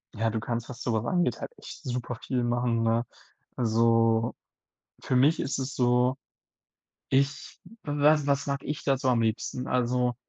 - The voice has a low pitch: Yes, low, 125 Hz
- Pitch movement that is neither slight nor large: Yes, average, 3.0 semitones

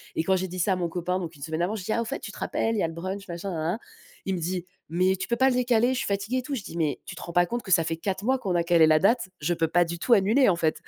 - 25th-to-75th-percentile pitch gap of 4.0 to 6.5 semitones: Yes, average, 4.3 semitones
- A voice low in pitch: No, medium, 185 Hz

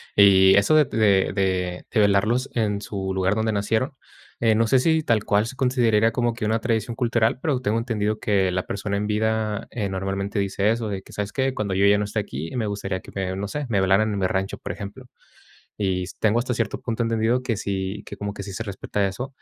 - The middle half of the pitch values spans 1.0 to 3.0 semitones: Yes, narrow, 2.6 semitones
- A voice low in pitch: Yes, low, 105 Hz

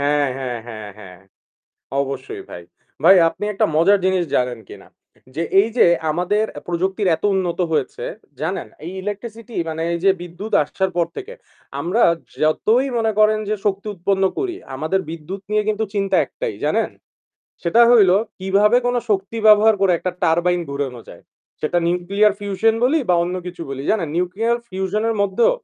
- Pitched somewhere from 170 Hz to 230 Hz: Yes, high, 190 Hz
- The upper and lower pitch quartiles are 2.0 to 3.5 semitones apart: No, average, 4.2 semitones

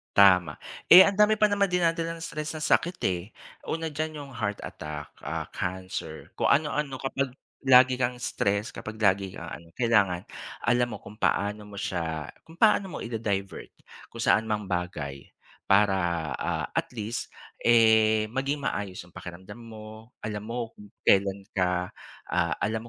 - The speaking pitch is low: Yes, low, 110 Hz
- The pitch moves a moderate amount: No, wide, 5.9 semitones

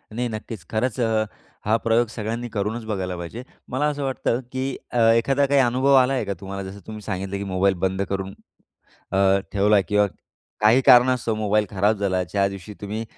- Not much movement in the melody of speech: No, average, 3.7 semitones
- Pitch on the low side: Yes, low, 110 Hz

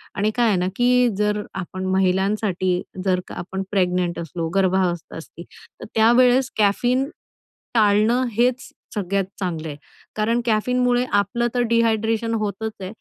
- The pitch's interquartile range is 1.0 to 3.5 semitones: No, average, 4.1 semitones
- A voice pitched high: Yes, high, 210 Hz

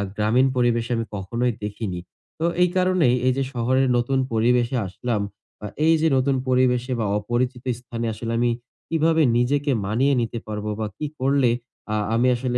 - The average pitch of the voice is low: Yes, low, 125 Hz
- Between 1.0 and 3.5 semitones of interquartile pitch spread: Yes, narrow, 2.5 semitones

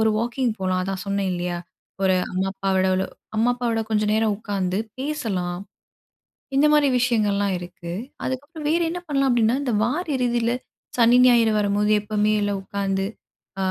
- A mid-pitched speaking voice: No, high, 215 Hz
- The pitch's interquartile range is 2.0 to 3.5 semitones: No, average, 4.2 semitones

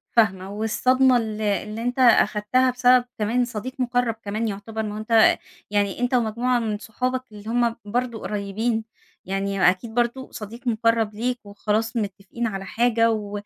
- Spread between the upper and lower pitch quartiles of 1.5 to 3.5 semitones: Yes, narrow, 2.6 semitones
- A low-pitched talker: No, high, 225 Hz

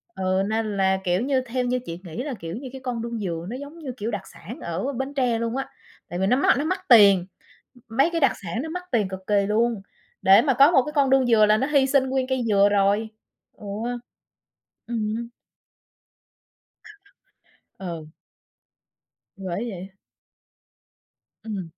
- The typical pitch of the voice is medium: No, high, 230 Hz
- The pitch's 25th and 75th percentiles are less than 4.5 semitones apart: No, average, 5.1 semitones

